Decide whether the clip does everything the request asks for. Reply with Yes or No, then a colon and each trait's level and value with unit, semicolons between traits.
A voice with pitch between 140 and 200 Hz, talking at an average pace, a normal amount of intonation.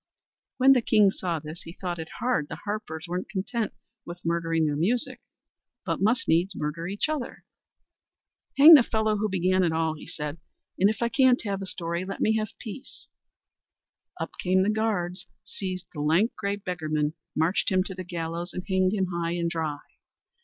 Yes: medium, 185 Hz; average, 185 wpm; average, 4.2 semitones